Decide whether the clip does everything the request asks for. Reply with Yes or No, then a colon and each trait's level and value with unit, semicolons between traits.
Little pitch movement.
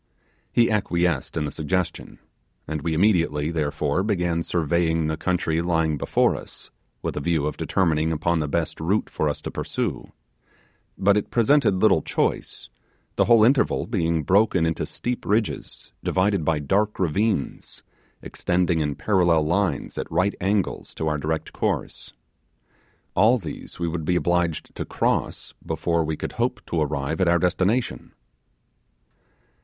No: average, 3.6 semitones